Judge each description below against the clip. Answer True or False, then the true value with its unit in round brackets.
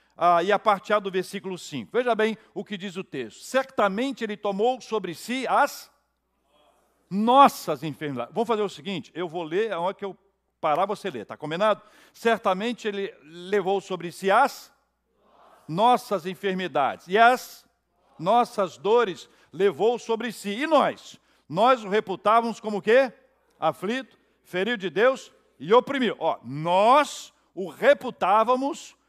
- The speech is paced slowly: False (145 wpm)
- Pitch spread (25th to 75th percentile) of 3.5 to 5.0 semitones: True (4.3 semitones)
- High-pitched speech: True (210 Hz)